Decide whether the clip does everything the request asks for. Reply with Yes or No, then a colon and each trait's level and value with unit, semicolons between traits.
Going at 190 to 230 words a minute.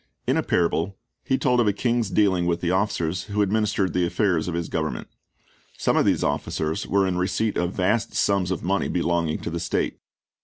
Yes: average, 200 wpm